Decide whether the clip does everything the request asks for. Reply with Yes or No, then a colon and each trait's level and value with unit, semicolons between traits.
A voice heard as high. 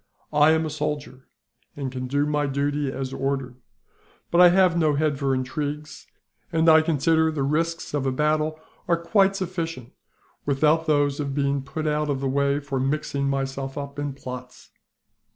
No: medium, 145 Hz